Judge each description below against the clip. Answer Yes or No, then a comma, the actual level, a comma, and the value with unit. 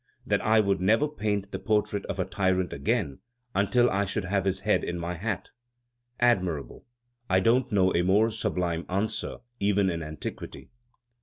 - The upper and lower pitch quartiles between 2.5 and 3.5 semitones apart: Yes, average, 2.8 semitones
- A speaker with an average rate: Yes, average, 165 wpm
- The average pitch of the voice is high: No, low, 100 Hz